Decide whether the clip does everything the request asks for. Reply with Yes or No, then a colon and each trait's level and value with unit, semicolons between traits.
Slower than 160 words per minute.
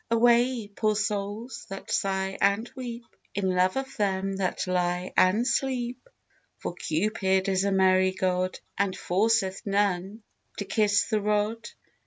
Yes: average, 140 wpm